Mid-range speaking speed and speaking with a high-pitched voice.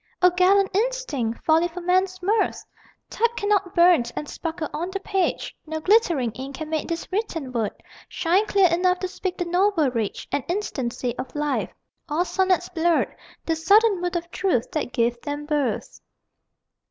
Yes: average, 165 wpm; very high, 345 Hz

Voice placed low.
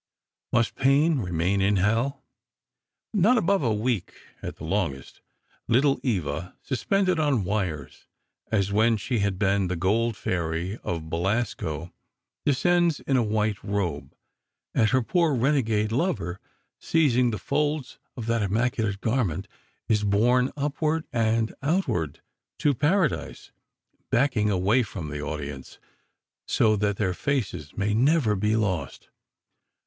Yes: low, 110 Hz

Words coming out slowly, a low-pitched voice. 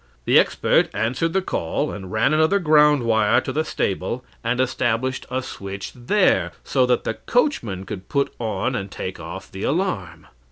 No: average, 170 wpm; low, 120 Hz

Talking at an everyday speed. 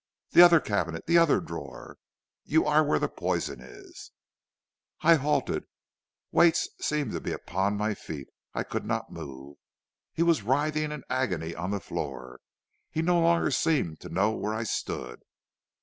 Yes: average, 160 wpm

